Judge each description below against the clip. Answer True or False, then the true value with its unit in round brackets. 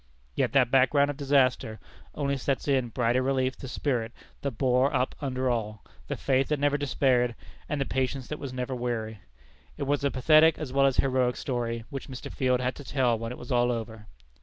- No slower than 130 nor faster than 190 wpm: False (205 wpm)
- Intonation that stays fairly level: True (2.2 semitones)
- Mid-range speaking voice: False (130 Hz)